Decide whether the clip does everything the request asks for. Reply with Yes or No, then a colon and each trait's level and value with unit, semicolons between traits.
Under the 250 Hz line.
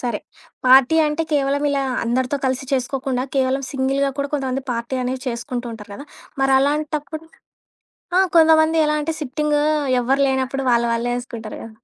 No: very high, 270 Hz